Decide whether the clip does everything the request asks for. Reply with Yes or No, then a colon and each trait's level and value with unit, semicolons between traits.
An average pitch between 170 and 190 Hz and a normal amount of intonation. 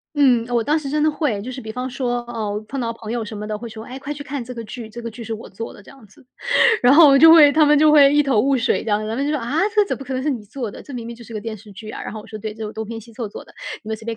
No: high, 235 Hz; average, 4.0 semitones